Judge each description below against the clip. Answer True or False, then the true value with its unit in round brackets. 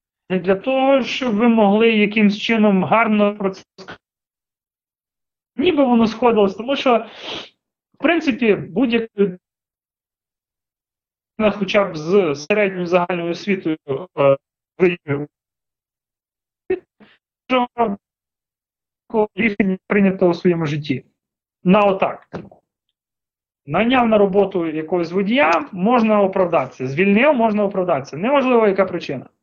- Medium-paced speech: False (100 wpm)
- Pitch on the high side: True (205 Hz)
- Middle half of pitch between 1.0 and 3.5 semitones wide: False (4.1 semitones)